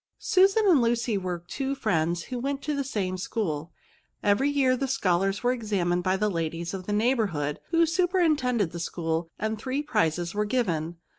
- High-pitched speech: Yes, high, 210 Hz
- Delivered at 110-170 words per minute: No, average, 180 wpm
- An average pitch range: No, wide, 7.3 semitones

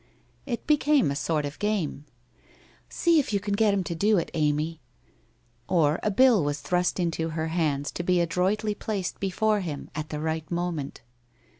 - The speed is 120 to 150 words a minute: No, average, 185 wpm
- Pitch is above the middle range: No, medium, 175 Hz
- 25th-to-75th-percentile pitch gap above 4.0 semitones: Yes, average, 5.0 semitones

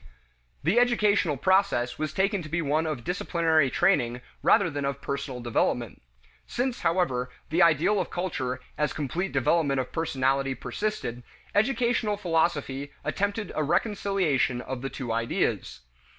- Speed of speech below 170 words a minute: Yes, slow, 135 wpm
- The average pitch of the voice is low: No, medium, 155 Hz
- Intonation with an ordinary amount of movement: No, wide, 6.3 semitones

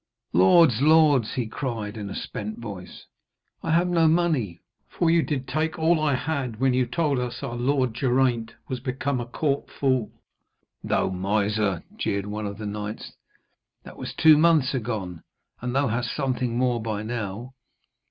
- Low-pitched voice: Yes, low, 125 Hz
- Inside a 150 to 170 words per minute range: Yes, average, 165 wpm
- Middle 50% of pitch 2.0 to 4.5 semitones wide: No, average, 4.9 semitones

